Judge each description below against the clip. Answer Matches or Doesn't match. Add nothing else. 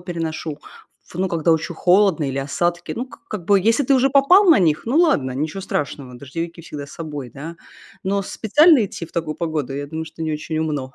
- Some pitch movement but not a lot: Matches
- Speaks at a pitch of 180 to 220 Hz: Doesn't match